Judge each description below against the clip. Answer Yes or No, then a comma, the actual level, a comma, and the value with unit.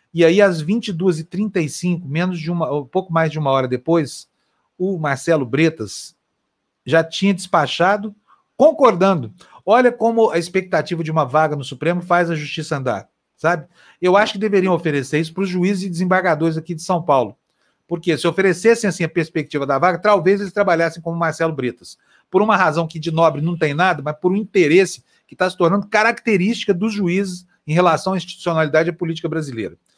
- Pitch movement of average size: Yes, average, 3.4 semitones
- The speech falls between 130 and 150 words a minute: No, fast, 185 wpm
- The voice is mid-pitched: Yes, medium, 175 Hz